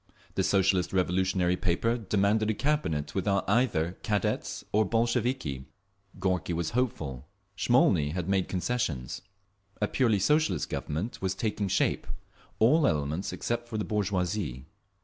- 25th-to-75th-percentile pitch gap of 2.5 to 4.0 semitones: No, average, 4.5 semitones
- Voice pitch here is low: Yes, very low, 95 Hz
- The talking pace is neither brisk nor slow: No, slow, 120 wpm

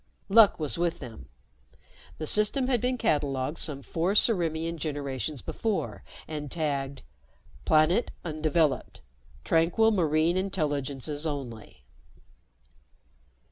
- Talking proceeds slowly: Yes, slow, 100 wpm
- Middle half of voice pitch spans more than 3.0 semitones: Yes, average, 4.0 semitones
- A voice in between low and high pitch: Yes, medium, 155 Hz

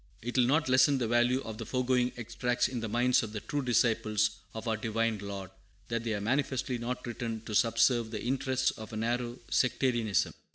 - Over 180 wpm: Yes, average, 200 wpm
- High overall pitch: No, low, 120 Hz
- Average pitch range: No, narrow, 2.3 semitones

